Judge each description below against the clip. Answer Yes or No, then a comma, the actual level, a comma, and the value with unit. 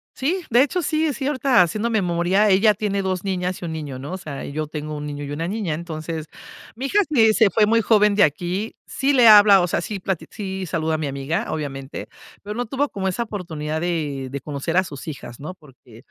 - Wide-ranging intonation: Yes, wide, 5.9 semitones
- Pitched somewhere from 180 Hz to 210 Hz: Yes, medium, 185 Hz